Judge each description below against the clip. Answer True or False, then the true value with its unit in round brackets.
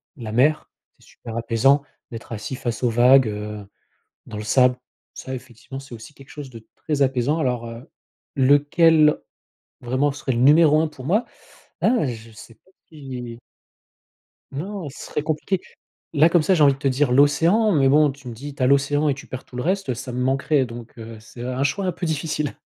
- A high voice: False (135 Hz)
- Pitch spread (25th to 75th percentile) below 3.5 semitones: False (3.8 semitones)